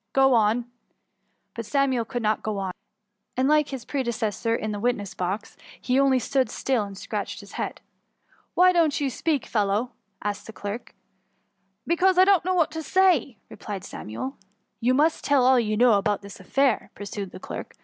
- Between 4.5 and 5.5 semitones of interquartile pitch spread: Yes, average, 5.1 semitones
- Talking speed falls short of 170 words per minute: No, average, 195 wpm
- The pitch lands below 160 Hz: No, high, 240 Hz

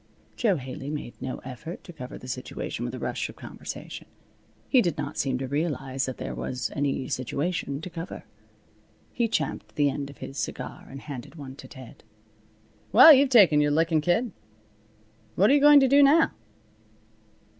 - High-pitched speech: No, medium, 150 Hz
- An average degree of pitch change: No, wide, 5.9 semitones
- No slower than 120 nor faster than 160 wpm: No, average, 175 wpm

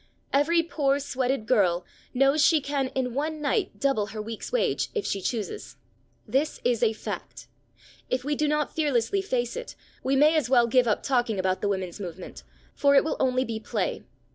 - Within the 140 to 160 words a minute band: No, average, 190 wpm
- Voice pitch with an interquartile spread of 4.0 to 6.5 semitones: Yes, average, 4.7 semitones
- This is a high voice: Yes, very high, 260 Hz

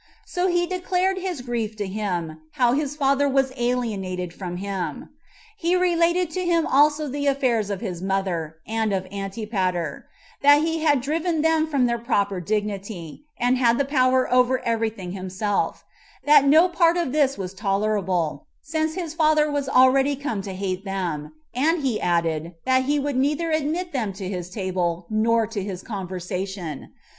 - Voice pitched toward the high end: Yes, high, 235 Hz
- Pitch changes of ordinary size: No, wide, 7.4 semitones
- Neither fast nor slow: Yes, average, 170 wpm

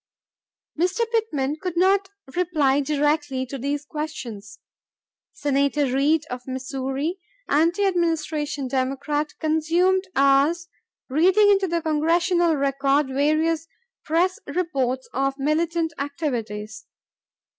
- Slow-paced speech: Yes, slow, 100 wpm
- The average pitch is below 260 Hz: No, very high, 300 Hz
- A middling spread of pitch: Yes, average, 3.8 semitones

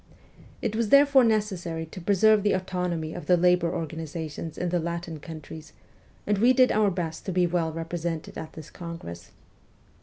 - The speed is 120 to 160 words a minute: No, average, 170 wpm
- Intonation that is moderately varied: Yes, average, 3.4 semitones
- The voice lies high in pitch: No, medium, 175 Hz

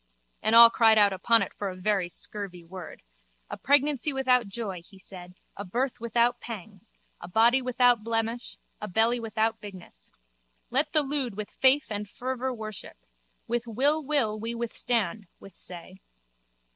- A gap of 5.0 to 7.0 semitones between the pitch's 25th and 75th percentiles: No, average, 3.7 semitones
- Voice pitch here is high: Yes, high, 225 Hz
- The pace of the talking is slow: No, average, 155 wpm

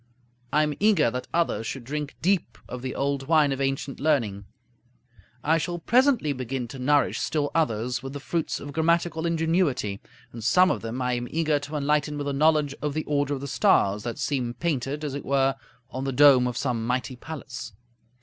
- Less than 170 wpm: No, average, 195 wpm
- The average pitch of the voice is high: No, medium, 140 Hz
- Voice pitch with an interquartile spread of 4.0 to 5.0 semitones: No, average, 3.6 semitones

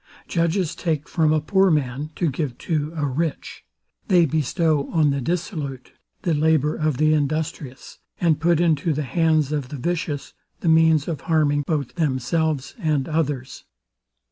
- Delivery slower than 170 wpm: Yes, average, 155 wpm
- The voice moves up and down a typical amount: No, narrow, 2.3 semitones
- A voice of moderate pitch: Yes, medium, 155 Hz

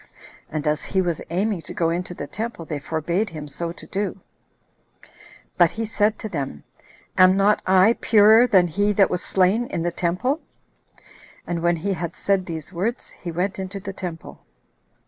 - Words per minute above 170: Yes, average, 180 wpm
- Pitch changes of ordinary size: Yes, average, 3.3 semitones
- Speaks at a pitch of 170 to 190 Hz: Yes, medium, 185 Hz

